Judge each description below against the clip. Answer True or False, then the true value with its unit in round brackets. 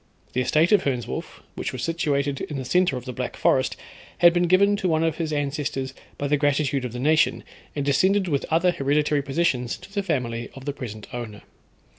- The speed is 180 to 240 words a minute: True (205 wpm)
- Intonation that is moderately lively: True (4.1 semitones)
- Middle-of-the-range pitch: True (145 Hz)